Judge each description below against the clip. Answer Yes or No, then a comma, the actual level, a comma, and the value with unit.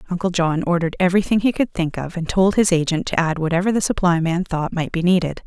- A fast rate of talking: Yes, fast, 240 wpm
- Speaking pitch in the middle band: Yes, medium, 175 Hz